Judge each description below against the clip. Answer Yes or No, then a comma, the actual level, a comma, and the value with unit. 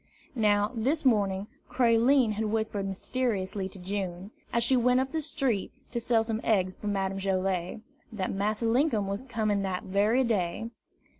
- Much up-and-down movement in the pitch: No, average, 3.5 semitones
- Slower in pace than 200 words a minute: Yes, average, 160 wpm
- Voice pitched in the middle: No, high, 215 Hz